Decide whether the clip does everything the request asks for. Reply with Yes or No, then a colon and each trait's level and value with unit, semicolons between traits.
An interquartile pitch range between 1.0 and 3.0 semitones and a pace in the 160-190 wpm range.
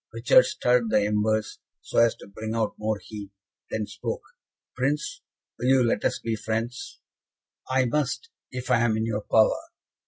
Yes: narrow, 2.6 semitones; average, 165 wpm